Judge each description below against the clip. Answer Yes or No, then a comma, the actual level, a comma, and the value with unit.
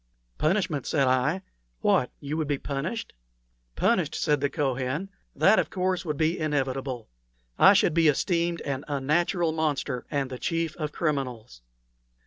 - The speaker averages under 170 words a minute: Yes, average, 145 wpm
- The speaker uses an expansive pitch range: No, average, 3.6 semitones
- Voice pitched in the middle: Yes, medium, 150 Hz